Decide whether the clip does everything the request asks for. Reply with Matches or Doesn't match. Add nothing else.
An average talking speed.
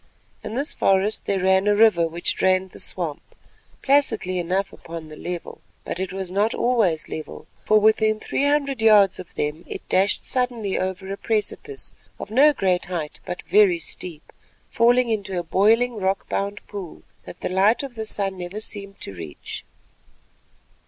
Matches